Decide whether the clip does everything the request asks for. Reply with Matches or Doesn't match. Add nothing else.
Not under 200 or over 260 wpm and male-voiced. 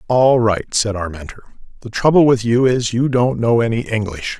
Matches